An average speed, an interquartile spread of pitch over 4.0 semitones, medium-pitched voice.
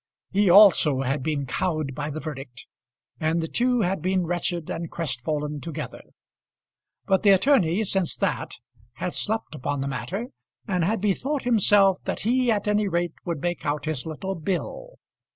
Yes: average, 165 wpm; average, 5.1 semitones; medium, 175 Hz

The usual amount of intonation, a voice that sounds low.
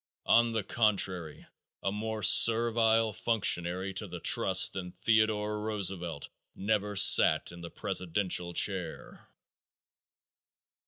Yes: average, 3.5 semitones; low, 100 Hz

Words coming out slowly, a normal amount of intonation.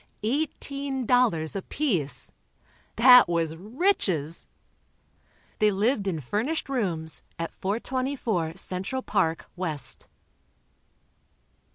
No: slow, 80 wpm; wide, 7.6 semitones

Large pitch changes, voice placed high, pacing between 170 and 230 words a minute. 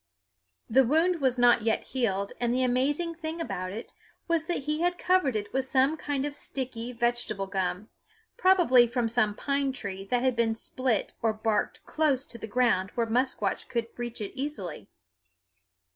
No: average, 4.0 semitones; high, 245 Hz; average, 175 wpm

